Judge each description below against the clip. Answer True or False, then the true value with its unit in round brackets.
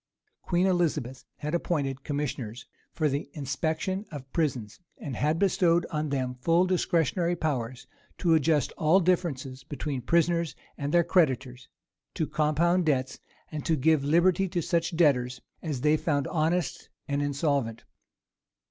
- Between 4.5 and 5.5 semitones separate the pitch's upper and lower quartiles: False (3.9 semitones)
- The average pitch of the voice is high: False (150 Hz)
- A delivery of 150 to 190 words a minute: False (140 wpm)